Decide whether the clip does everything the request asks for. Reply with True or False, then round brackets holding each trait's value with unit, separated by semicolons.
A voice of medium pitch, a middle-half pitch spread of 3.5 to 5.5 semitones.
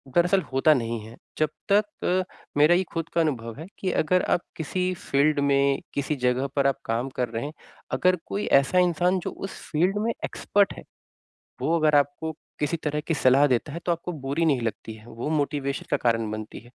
True (150 Hz; 4.6 semitones)